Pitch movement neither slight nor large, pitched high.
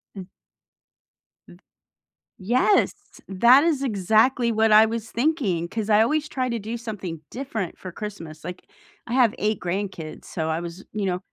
Yes: average, 4.4 semitones; high, 215 Hz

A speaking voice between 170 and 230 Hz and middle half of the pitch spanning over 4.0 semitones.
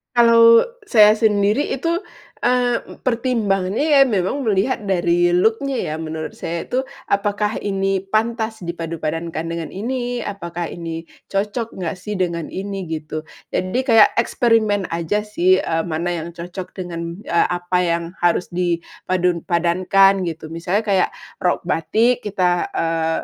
Yes: high, 190 Hz; average, 4.4 semitones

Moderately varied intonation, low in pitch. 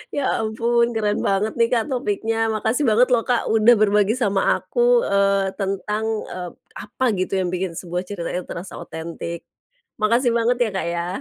No: average, 3.4 semitones; high, 215 Hz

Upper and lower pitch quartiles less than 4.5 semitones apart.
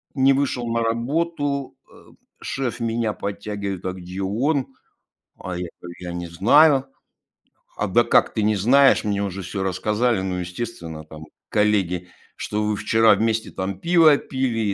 No: average, 5.0 semitones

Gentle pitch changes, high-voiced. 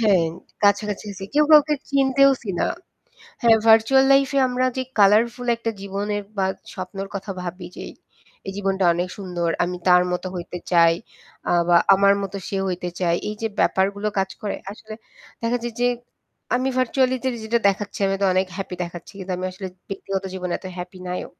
No: average, 3.8 semitones; high, 200 Hz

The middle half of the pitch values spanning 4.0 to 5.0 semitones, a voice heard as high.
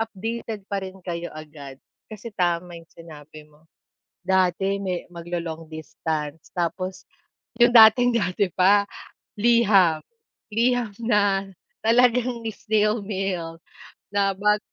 Yes: average, 4.4 semitones; high, 195 Hz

